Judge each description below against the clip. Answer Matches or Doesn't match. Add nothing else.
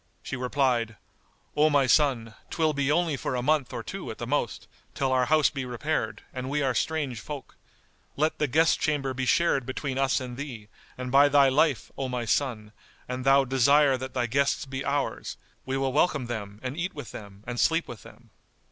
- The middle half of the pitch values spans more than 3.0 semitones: Doesn't match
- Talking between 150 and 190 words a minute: Doesn't match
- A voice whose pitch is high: Doesn't match